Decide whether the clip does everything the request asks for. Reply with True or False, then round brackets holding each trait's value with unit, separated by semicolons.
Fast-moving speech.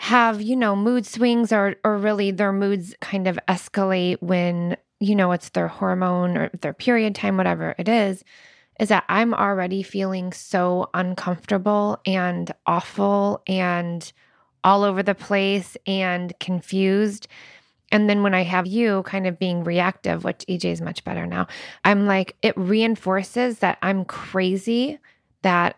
False (155 wpm)